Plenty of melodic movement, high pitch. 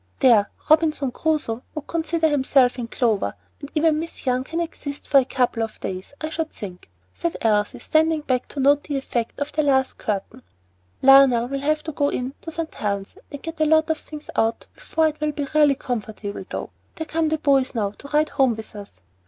No: average, 4.7 semitones; very high, 280 Hz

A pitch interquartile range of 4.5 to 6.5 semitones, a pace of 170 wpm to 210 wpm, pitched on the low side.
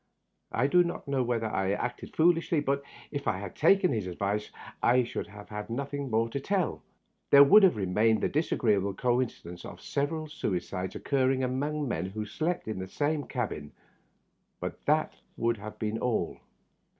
Yes: wide, 5.4 semitones; average, 175 wpm; low, 120 Hz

